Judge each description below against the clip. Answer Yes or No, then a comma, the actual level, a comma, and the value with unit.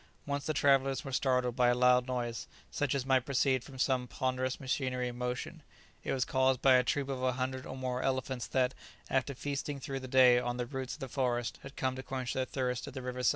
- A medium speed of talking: No, fast, 240 wpm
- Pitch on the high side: No, low, 130 Hz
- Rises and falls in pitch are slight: Yes, narrow, 1.1 semitones